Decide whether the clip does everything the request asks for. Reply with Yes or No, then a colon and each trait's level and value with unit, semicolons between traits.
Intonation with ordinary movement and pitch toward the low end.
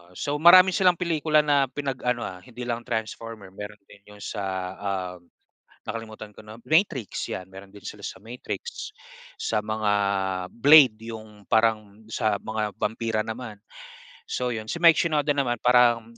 Yes: average, 4.8 semitones; low, 115 Hz